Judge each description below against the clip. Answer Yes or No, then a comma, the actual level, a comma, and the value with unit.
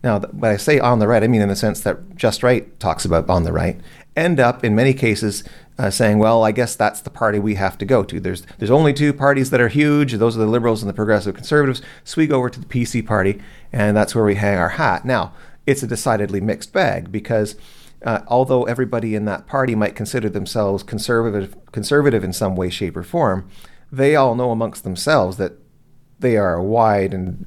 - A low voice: Yes, low, 110 Hz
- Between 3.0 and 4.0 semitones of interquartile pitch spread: Yes, average, 3.7 semitones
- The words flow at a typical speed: No, fast, 225 wpm